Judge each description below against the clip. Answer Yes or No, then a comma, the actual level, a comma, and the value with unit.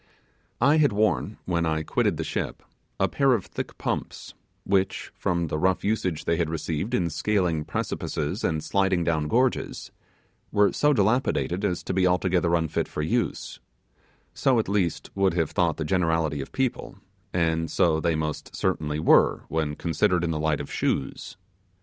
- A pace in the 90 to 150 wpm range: No, average, 170 wpm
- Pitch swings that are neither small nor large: Yes, average, 3.9 semitones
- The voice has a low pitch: Yes, very low, 85 Hz